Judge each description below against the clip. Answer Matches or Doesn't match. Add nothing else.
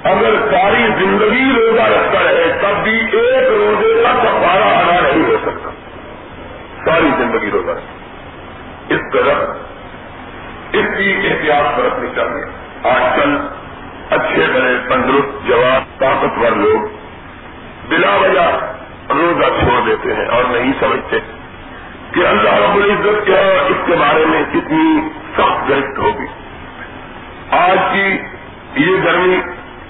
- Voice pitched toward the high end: Matches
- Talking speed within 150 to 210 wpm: Doesn't match